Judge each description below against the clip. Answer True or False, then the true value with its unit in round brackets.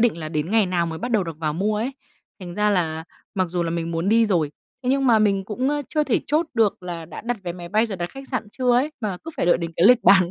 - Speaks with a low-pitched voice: False (200 Hz)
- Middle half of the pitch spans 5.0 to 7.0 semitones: True (5.5 semitones)